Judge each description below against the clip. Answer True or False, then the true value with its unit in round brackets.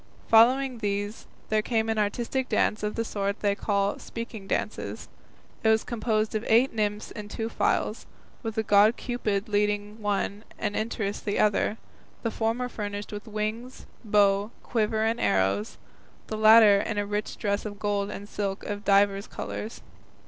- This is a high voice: True (210 Hz)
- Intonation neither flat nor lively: False (1.5 semitones)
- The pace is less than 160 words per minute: False (165 wpm)